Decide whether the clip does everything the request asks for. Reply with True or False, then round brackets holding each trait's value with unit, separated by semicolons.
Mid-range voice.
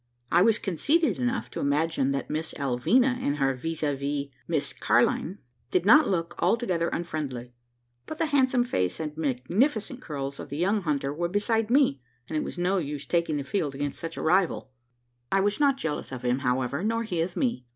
True (165 Hz)